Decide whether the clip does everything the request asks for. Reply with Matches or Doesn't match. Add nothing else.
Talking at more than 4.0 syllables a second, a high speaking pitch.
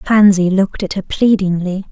Matches